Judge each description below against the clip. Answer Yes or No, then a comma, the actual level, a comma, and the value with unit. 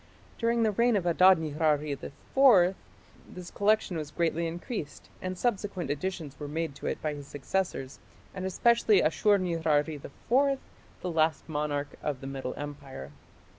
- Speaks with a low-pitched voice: No, medium, 165 Hz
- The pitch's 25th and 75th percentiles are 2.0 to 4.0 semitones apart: No, average, 4.7 semitones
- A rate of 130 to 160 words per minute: Yes, average, 150 wpm